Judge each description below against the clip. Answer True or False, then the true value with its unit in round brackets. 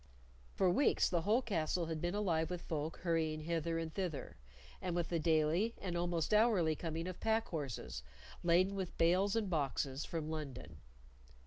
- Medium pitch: True (170 Hz)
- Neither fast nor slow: True (165 wpm)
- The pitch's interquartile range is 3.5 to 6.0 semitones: False (2.8 semitones)